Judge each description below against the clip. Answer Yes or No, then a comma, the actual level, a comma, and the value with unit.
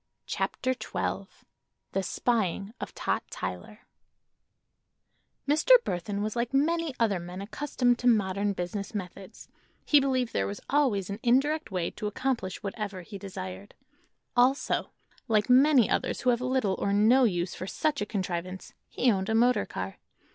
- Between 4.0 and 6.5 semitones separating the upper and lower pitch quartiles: Yes, average, 4.9 semitones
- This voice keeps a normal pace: Yes, average, 150 wpm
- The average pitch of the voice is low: No, high, 215 Hz